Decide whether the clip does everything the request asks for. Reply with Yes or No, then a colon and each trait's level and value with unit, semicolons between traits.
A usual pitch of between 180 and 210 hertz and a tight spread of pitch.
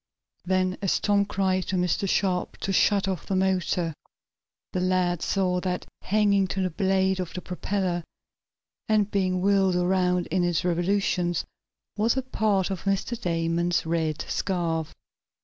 Yes: medium, 185 Hz; narrow, 1.8 semitones